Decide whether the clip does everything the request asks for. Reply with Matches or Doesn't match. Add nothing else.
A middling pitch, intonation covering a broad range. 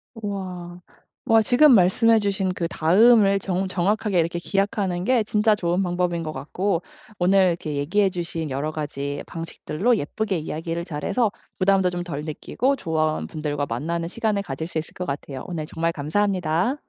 Doesn't match